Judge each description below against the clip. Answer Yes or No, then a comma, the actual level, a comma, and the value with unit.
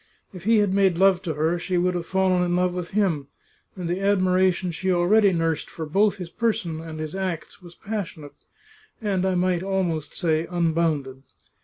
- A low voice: No, medium, 180 Hz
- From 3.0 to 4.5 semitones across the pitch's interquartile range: No, narrow, 2.5 semitones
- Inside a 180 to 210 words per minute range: Yes, average, 185 wpm